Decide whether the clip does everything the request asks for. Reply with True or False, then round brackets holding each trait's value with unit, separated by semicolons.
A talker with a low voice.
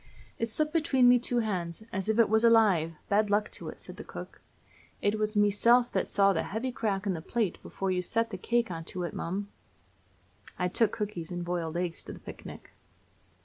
False (205 Hz)